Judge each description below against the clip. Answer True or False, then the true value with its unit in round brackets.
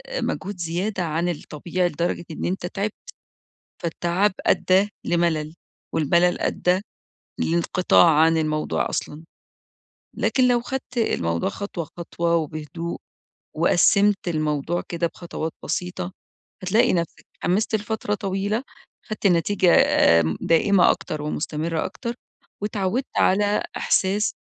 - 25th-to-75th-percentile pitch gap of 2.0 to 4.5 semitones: True (3.7 semitones)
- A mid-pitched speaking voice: True (175 Hz)